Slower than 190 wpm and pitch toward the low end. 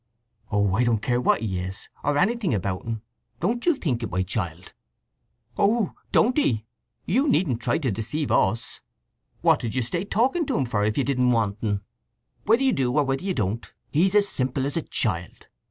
No: average, 200 wpm; low, 125 Hz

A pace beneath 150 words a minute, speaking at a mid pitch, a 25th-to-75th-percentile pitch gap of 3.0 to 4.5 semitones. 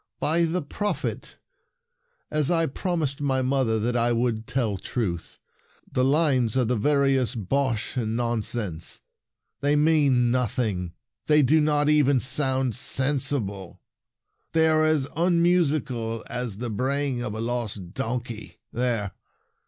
No: slow, 135 wpm; low, 130 Hz; average, 4.2 semitones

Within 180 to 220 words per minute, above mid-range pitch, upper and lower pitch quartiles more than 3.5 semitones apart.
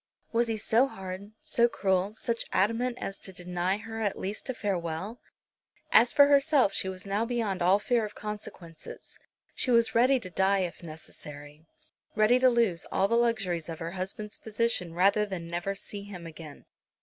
Yes: average, 185 wpm; high, 200 Hz; average, 4.2 semitones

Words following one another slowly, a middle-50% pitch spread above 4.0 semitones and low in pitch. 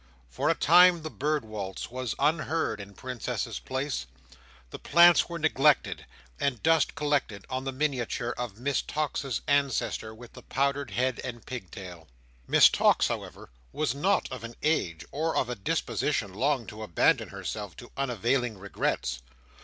No: average, 155 wpm; average, 5.3 semitones; low, 130 Hz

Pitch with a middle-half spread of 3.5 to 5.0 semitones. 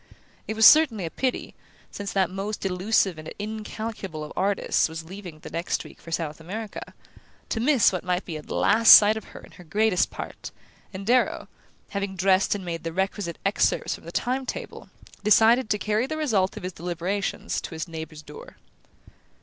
Yes: average, 4.0 semitones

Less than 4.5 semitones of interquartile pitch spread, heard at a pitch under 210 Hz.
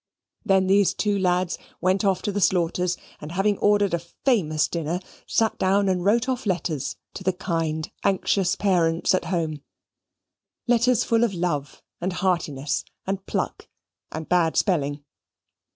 Yes: average, 3.2 semitones; medium, 185 Hz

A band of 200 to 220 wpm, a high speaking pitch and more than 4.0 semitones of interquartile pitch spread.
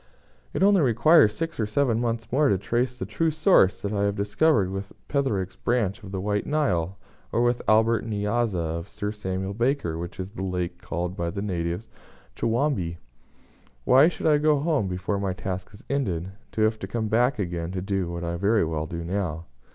No: fast, 205 wpm; low, 105 Hz; average, 4.7 semitones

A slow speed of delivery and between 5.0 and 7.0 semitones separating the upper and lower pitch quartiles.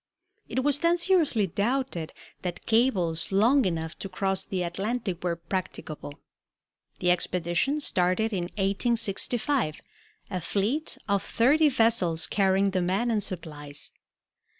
Yes: slow, 125 wpm; wide, 5.4 semitones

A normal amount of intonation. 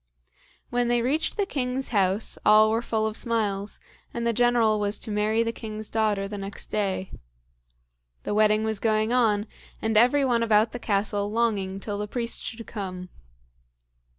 No: narrow, 2.2 semitones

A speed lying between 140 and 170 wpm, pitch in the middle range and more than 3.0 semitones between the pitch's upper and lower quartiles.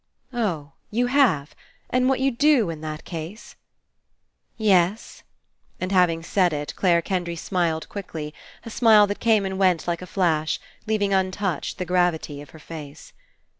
Yes: average, 160 wpm; medium, 180 Hz; average, 4.4 semitones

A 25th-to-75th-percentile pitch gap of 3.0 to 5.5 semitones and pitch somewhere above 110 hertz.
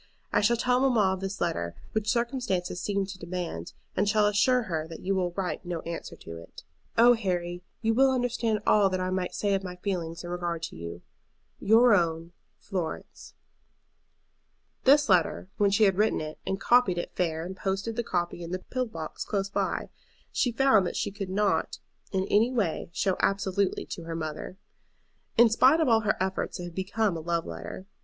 Yes: average, 4.0 semitones; high, 190 Hz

